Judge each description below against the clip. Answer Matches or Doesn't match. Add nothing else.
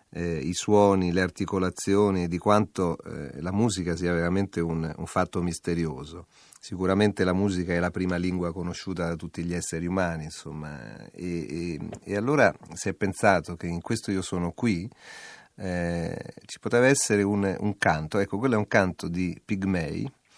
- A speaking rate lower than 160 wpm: Doesn't match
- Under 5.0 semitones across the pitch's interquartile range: Matches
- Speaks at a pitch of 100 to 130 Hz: Doesn't match